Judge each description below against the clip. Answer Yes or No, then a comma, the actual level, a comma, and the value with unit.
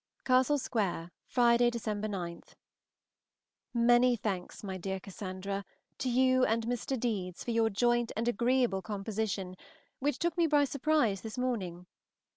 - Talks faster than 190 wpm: No, slow, 135 wpm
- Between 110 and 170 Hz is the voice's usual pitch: No, high, 230 Hz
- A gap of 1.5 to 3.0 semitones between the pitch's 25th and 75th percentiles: No, average, 4.2 semitones